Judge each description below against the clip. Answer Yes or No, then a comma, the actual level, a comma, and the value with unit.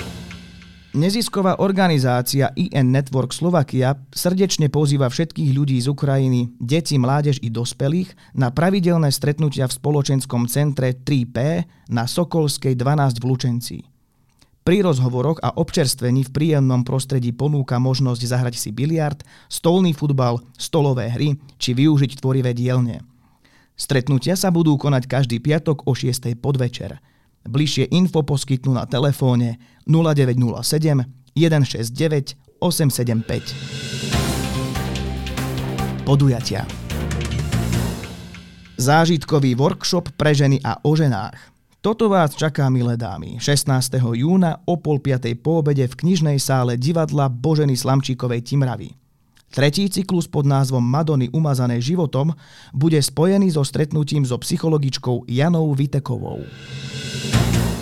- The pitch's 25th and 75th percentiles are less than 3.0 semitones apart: No, average, 3.7 semitones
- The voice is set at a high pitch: No, low, 135 Hz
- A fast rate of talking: No, slow, 110 wpm